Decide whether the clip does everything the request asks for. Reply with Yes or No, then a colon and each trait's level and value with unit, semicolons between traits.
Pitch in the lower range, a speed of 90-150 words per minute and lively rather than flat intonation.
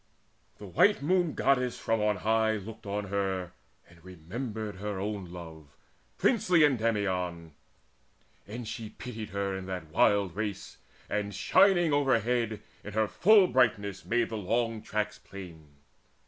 No: low, 105 Hz; slow, 135 wpm; average, 4.0 semitones